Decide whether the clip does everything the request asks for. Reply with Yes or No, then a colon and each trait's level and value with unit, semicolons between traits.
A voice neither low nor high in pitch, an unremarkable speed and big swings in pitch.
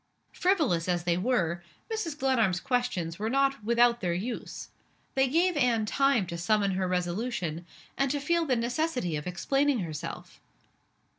No: high, 235 Hz; average, 150 wpm; wide, 7.4 semitones